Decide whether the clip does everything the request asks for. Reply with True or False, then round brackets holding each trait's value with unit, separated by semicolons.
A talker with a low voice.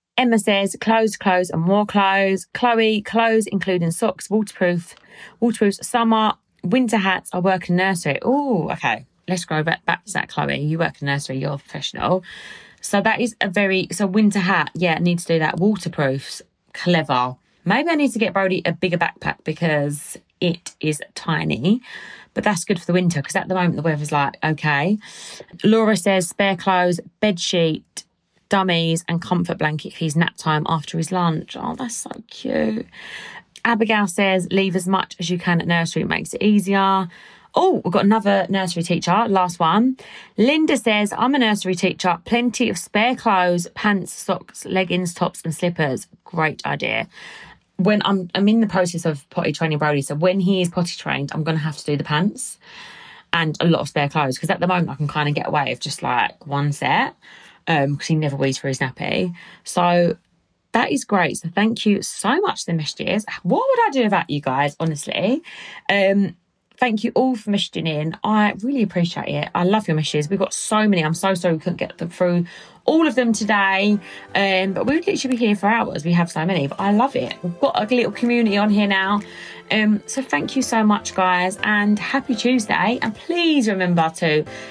False (190 Hz)